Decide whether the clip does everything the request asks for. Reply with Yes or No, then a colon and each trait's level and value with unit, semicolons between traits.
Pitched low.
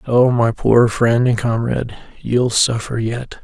Yes: low, 120 Hz